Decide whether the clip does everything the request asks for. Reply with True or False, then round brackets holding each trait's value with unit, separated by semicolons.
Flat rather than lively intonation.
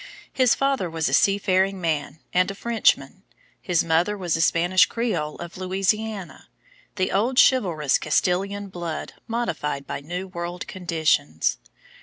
False (3.6 semitones)